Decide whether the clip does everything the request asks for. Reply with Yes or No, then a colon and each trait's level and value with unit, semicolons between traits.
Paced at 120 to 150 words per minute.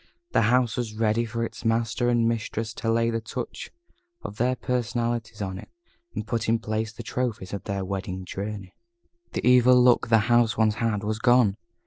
No: average, 185 wpm